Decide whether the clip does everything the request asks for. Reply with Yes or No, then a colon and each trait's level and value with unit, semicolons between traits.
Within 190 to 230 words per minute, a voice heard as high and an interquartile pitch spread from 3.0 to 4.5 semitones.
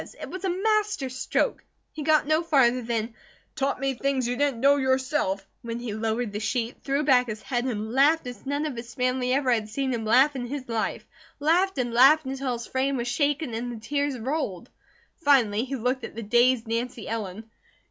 Yes: fast, 205 wpm; very high, 255 Hz; average, 3.4 semitones